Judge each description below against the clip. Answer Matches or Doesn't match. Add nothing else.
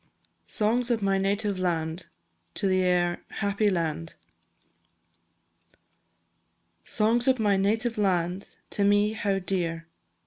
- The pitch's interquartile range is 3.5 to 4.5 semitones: Doesn't match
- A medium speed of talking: Doesn't match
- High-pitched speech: Matches